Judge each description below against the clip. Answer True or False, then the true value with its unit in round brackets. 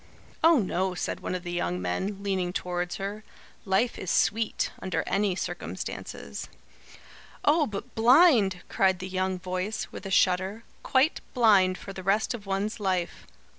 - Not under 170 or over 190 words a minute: False (155 wpm)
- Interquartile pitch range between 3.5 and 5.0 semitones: False (2.7 semitones)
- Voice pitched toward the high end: True (195 Hz)